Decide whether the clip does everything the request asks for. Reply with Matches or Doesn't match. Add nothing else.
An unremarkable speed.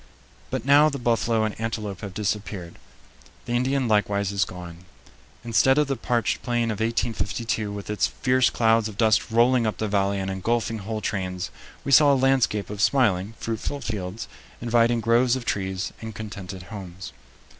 Matches